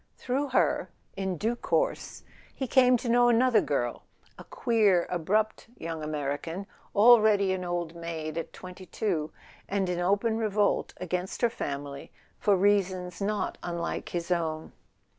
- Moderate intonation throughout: Yes, average, 4.5 semitones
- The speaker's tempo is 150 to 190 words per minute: No, average, 140 wpm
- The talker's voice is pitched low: No, high, 190 Hz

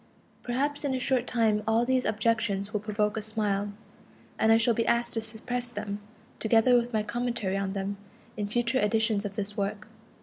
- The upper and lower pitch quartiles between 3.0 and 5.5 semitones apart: No, narrow, 2.6 semitones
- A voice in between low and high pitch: No, high, 220 Hz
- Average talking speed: Yes, average, 190 wpm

